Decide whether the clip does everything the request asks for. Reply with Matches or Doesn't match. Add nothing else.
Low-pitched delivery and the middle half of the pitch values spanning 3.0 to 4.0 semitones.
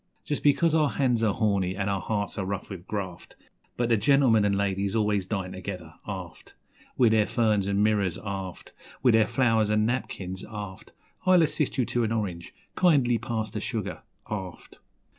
Matches